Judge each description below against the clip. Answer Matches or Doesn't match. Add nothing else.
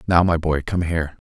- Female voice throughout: Doesn't match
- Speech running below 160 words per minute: Doesn't match